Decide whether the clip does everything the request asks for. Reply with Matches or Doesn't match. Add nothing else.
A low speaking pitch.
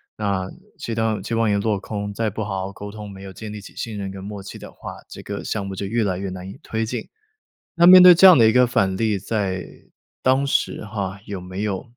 Matches